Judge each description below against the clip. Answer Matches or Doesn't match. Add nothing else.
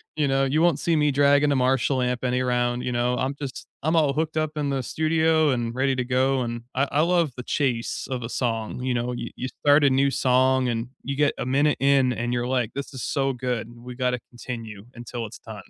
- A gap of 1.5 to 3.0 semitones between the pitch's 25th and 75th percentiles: Matches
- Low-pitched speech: Matches